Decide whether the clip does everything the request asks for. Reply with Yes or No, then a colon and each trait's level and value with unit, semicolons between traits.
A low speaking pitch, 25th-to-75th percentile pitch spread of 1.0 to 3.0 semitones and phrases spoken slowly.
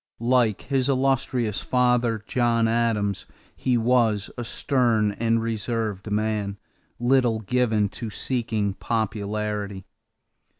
Yes: low, 115 Hz; narrow, 2.6 semitones; slow, 100 wpm